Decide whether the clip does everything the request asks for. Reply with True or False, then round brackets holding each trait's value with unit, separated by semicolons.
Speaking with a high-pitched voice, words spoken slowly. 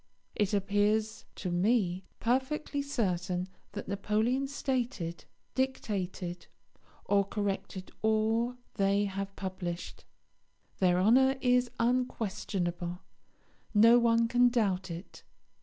True (205 Hz; 95 wpm)